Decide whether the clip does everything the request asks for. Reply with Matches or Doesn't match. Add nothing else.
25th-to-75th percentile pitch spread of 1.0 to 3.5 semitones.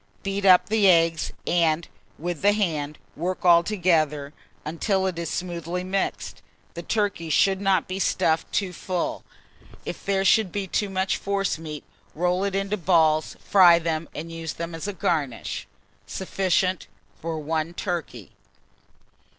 Matches